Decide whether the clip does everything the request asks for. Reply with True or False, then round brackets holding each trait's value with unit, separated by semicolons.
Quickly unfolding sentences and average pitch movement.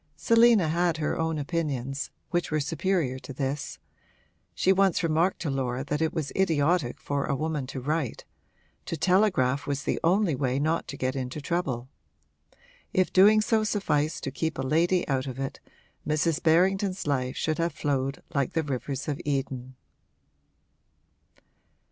False (155 wpm; 4.1 semitones)